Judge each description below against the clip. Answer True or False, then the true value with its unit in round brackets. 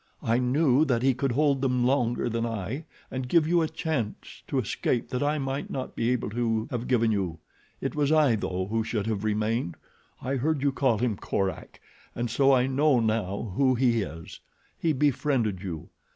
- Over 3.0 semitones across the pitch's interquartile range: True (3.7 semitones)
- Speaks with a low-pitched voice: True (125 Hz)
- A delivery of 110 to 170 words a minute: False (195 wpm)